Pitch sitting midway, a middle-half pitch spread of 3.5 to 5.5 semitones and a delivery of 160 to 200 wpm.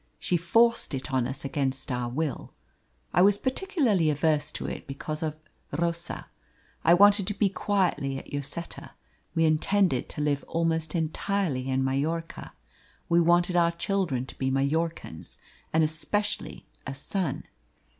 No: medium, 160 Hz; average, 4.6 semitones; average, 145 wpm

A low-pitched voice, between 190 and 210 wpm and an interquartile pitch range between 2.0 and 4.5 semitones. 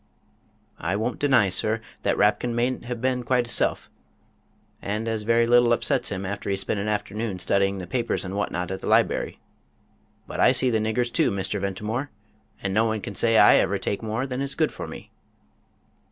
Yes: low, 110 Hz; average, 195 wpm; average, 3.5 semitones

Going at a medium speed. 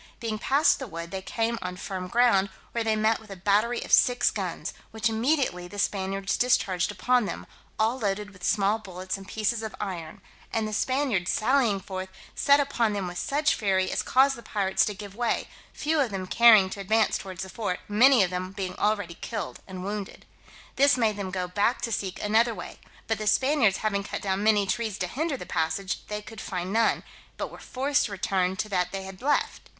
No: fast, 210 wpm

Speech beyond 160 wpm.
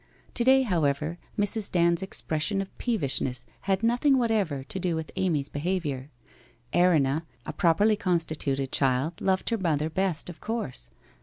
No: average, 145 wpm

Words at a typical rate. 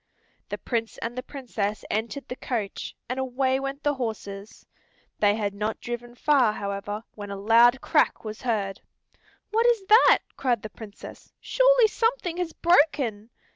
Yes: average, 155 wpm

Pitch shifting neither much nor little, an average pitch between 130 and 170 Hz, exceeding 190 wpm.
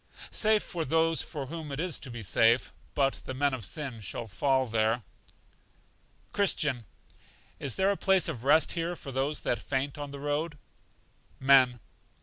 No: average, 4.3 semitones; medium, 140 Hz; average, 165 wpm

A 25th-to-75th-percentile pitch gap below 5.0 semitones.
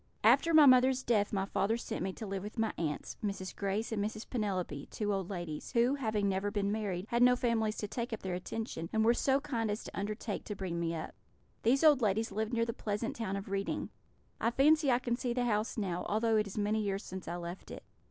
Yes: average, 3.2 semitones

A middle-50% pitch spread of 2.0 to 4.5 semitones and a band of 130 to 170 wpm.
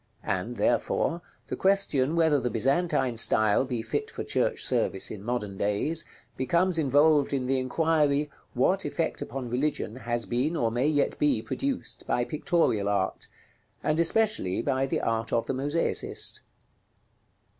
No: average, 5.1 semitones; average, 145 wpm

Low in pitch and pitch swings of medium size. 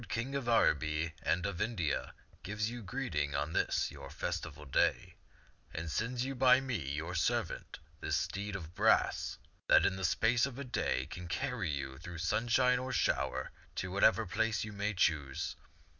No: very low, 95 Hz; wide, 7.0 semitones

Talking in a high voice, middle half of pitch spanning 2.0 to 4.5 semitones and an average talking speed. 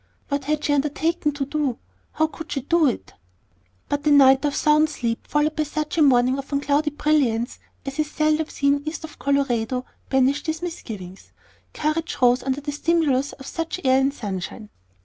Yes: very high, 285 Hz; narrow, 2.6 semitones; average, 180 wpm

